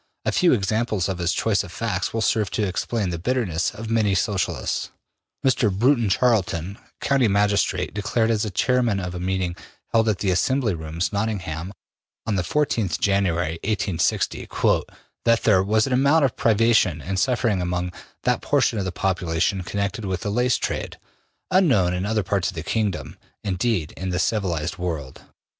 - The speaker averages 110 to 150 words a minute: No, average, 165 wpm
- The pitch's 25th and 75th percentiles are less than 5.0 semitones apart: Yes, average, 4.0 semitones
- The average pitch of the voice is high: No, low, 100 Hz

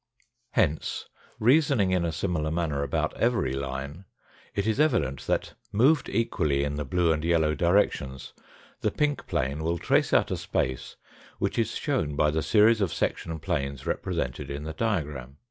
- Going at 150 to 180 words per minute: Yes, average, 165 wpm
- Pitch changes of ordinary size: No, wide, 6.3 semitones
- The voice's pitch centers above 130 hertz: No, very low, 80 Hz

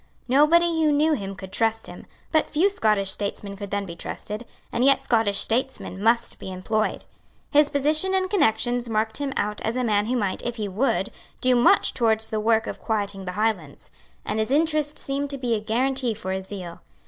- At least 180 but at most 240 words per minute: Yes, average, 200 wpm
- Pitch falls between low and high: No, high, 225 Hz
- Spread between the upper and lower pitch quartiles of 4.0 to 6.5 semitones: Yes, average, 5.0 semitones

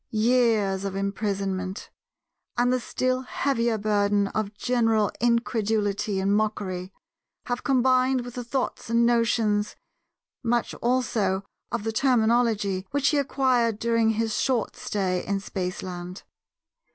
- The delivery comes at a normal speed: No, slow, 125 wpm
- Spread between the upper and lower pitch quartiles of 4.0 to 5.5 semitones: No, average, 3.5 semitones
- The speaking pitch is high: Yes, high, 225 Hz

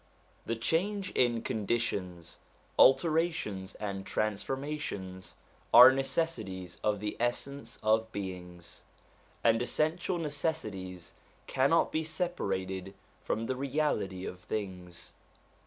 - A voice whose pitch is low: Yes, low, 110 Hz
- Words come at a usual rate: No, slow, 95 wpm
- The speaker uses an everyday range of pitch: No, wide, 7.4 semitones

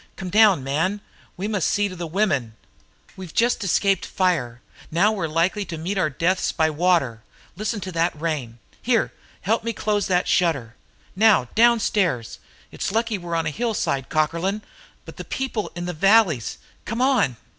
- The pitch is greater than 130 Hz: Yes, medium, 185 Hz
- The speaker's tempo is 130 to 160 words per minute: No, average, 175 wpm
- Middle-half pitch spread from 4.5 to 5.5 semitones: Yes, average, 4.9 semitones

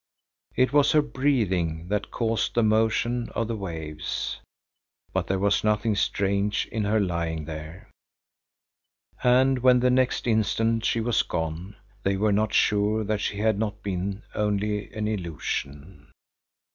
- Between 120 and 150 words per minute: Yes, average, 145 wpm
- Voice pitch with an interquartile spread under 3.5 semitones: Yes, average, 3.1 semitones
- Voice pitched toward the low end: Yes, low, 105 Hz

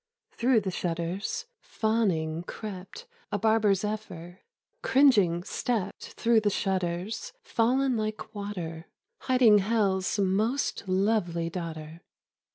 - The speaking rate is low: Yes, slow, 115 wpm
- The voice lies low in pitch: No, high, 200 Hz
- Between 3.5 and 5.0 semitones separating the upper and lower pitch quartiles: Yes, average, 4.1 semitones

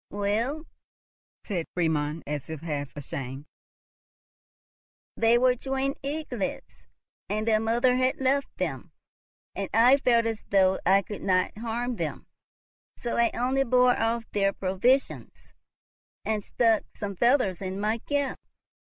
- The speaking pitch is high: Yes, high, 225 Hz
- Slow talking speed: Yes, slow, 130 wpm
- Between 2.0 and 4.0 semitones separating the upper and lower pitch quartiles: No, average, 4.7 semitones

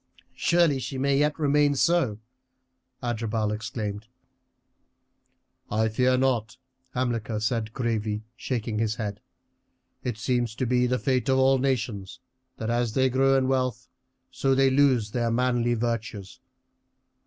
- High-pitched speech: No, low, 120 Hz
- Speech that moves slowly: Yes, slow, 130 wpm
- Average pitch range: Yes, average, 3.1 semitones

